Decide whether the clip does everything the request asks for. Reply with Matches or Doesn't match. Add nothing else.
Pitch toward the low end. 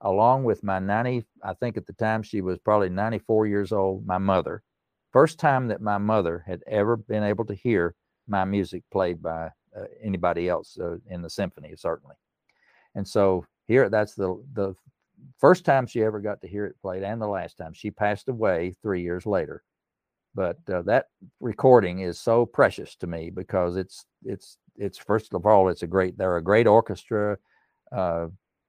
Matches